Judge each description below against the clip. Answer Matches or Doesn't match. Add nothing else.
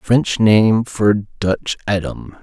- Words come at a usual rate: Doesn't match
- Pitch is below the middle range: Matches